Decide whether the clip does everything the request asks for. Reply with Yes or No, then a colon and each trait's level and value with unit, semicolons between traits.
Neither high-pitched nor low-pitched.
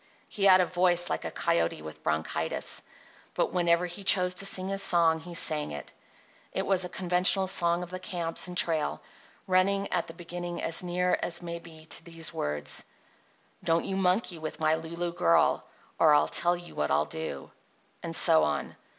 Yes: medium, 175 Hz